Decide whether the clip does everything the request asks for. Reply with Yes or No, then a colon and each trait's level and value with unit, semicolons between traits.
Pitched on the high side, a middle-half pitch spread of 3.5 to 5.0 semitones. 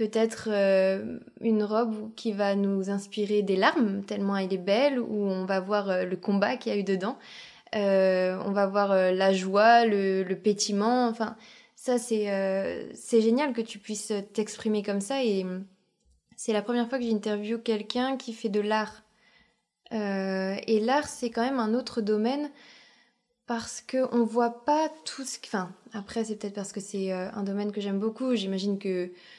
No: high, 215 Hz; average, 2.8 semitones